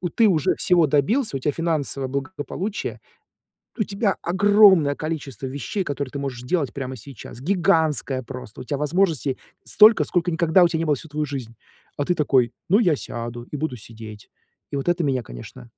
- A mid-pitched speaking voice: Yes, medium, 145 Hz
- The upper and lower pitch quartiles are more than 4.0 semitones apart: Yes, average, 5.0 semitones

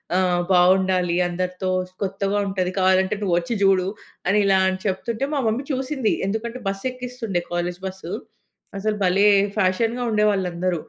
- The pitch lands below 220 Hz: Yes, high, 190 Hz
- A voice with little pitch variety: No, average, 3.0 semitones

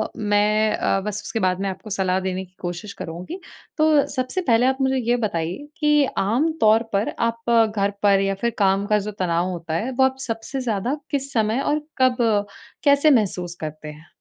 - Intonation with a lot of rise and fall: Yes, wide, 5.7 semitones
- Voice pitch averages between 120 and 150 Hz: No, high, 215 Hz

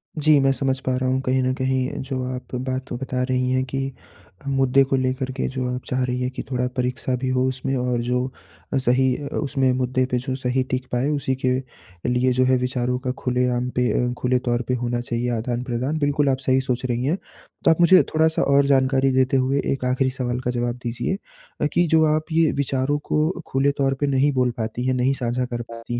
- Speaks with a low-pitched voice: Yes, low, 130 Hz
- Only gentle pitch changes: Yes, narrow, 1.2 semitones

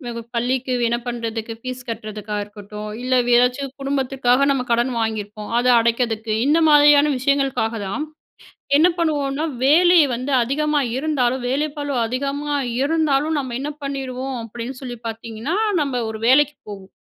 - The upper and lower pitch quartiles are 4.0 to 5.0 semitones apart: No, average, 3.6 semitones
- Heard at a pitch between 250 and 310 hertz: Yes, very high, 255 Hz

